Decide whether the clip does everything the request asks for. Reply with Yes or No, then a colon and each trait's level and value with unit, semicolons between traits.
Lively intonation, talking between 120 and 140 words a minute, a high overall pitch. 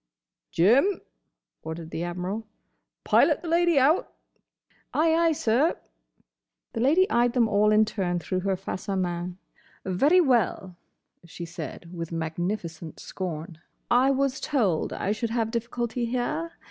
Yes: wide, 7.0 semitones; slow, 135 wpm; high, 215 Hz